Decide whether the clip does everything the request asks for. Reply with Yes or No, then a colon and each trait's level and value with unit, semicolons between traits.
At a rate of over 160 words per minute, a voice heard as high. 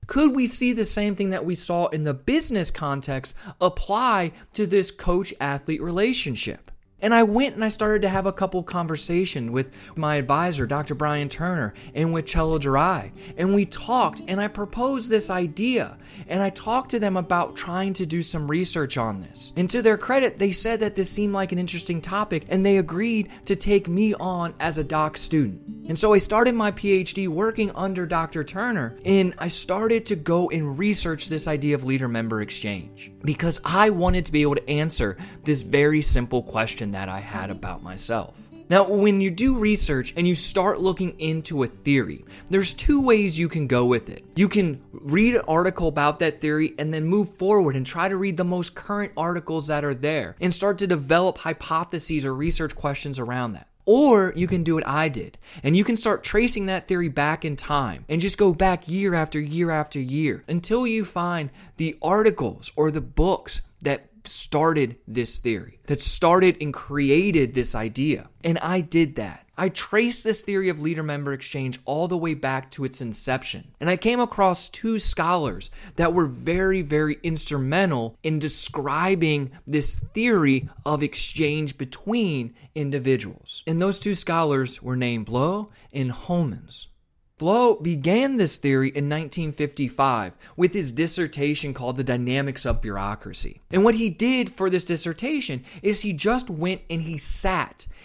No: average, 180 wpm; medium, 165 Hz